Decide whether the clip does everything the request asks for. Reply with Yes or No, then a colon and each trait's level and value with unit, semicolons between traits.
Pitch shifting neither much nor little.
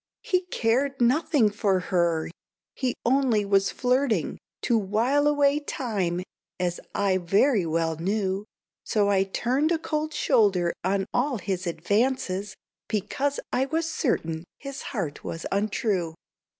No: wide, 6.3 semitones